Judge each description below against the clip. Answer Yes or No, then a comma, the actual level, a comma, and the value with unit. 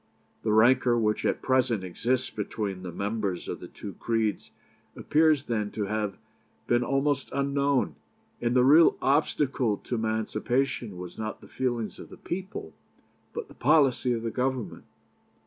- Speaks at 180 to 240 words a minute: No, average, 150 wpm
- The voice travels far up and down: No, average, 3.9 semitones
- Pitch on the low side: Yes, low, 120 Hz